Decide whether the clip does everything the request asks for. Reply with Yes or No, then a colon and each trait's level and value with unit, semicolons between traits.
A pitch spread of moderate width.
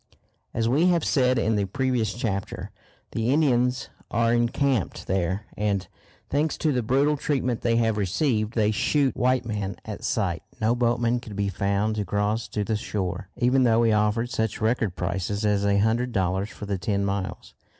Yes: average, 3.4 semitones